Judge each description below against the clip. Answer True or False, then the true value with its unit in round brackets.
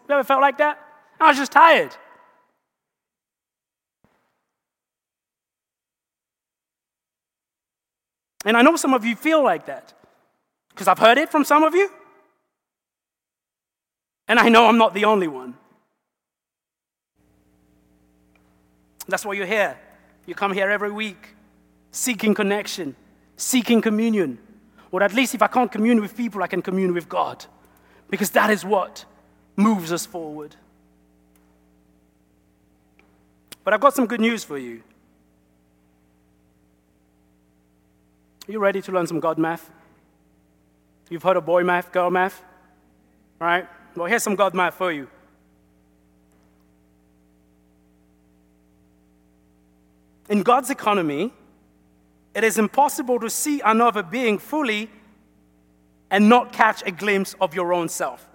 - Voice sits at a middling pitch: True (175 Hz)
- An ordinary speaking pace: False (125 wpm)